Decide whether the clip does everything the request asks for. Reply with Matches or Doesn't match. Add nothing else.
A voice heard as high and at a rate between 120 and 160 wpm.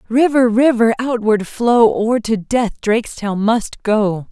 Matches